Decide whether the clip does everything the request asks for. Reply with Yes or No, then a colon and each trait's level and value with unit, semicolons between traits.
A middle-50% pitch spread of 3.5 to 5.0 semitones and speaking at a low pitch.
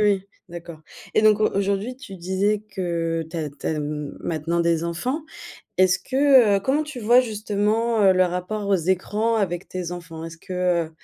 No: average, 4.0 semitones; high, 190 Hz